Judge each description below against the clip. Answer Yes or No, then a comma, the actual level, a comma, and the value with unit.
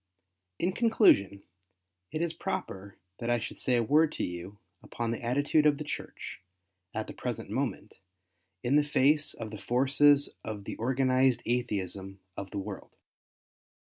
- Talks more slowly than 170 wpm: Yes, average, 155 wpm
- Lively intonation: Yes, wide, 6.0 semitones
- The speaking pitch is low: Yes, low, 125 Hz